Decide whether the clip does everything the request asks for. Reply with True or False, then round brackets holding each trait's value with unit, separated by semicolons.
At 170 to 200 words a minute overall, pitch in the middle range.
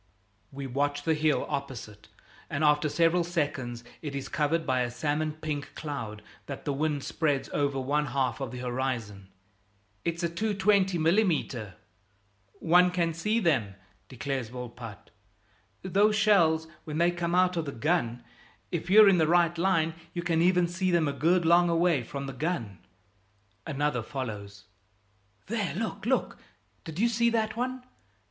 False (155 wpm; 155 Hz)